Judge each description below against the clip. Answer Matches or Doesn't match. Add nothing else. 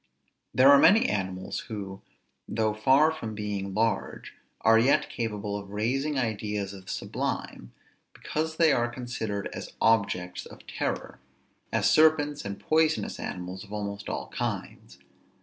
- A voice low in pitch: Matches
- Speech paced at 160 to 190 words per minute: Doesn't match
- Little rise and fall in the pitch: Doesn't match